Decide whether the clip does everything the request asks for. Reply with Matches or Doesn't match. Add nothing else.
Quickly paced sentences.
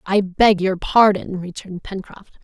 Doesn't match